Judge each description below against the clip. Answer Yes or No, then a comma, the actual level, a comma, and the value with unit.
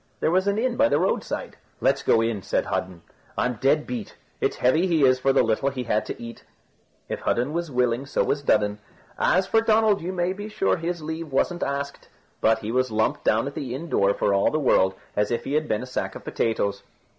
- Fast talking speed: Yes, fast, 230 wpm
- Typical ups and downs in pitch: No, wide, 7.1 semitones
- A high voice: No, low, 135 Hz